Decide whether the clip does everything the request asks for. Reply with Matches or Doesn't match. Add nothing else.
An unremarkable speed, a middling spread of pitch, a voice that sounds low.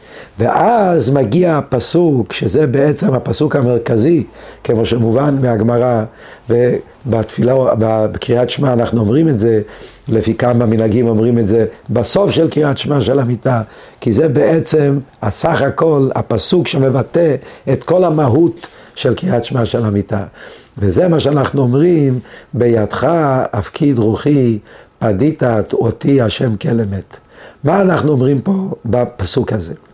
Matches